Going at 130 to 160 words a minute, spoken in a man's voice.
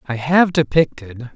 Yes: slow, 135 wpm; male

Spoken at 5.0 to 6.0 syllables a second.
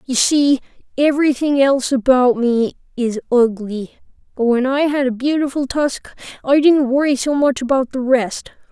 No: 4.7 syllables/s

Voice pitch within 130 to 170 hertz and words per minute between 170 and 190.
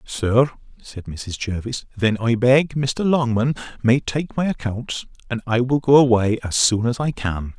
No: low, 120 Hz; average, 180 wpm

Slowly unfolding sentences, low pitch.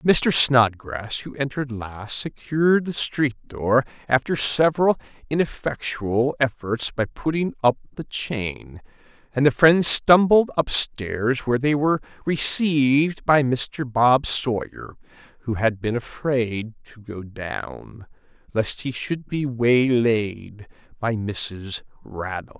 Yes: slow, 120 wpm; low, 125 Hz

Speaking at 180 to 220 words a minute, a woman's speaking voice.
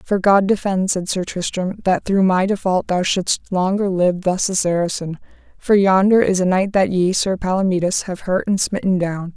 Yes: average, 200 wpm; female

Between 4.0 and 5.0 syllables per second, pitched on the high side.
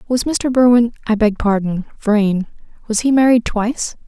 Yes: 4.7 syllables/s; high, 225 Hz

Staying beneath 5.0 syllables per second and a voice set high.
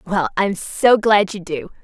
Yes: 4.6 syllables/s; high, 200 Hz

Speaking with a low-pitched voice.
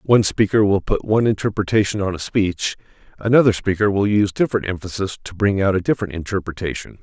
Yes: low, 100 Hz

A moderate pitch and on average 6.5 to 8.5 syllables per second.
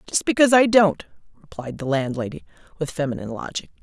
Yes: medium, 170 Hz; 6.6 syllables/s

